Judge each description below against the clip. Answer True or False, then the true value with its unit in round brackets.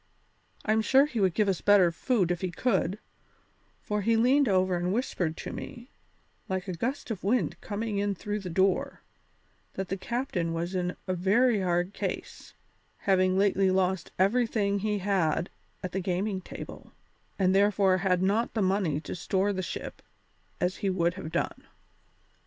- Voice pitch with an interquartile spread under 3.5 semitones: True (2.4 semitones)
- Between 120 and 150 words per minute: False (170 wpm)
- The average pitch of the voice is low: False (190 Hz)